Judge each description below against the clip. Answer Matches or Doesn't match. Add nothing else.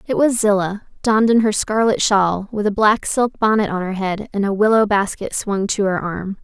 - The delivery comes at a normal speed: Doesn't match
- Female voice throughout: Matches